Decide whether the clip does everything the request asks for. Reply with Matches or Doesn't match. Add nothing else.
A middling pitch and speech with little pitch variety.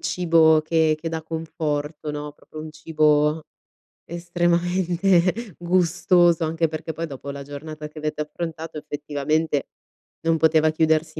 Matches